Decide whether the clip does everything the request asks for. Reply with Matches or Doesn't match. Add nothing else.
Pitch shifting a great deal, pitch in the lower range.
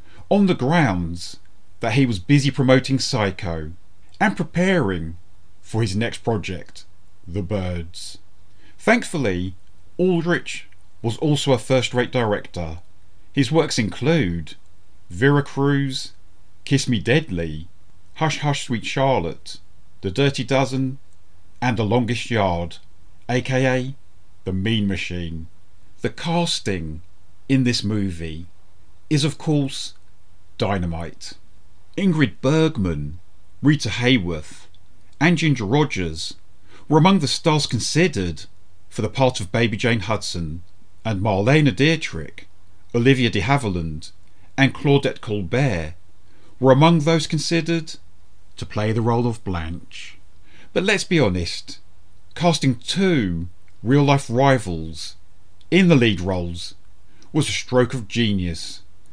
Matches